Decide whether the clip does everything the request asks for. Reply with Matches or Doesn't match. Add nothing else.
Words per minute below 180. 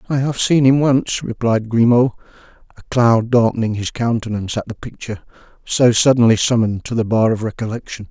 Matches